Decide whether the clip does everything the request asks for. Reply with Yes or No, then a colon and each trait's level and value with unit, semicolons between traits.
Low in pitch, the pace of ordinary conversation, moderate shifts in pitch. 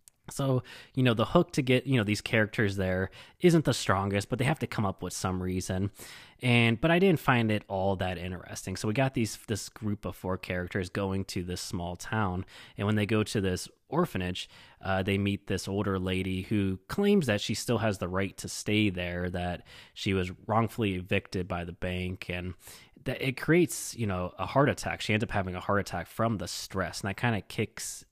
No: low, 100 Hz; fast, 220 wpm; average, 3.7 semitones